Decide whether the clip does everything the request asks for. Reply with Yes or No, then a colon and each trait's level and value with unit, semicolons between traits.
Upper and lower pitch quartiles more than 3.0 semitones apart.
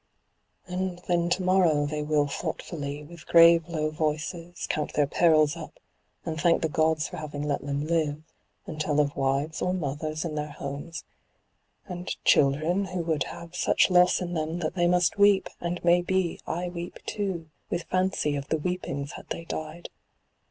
No: average, 2.7 semitones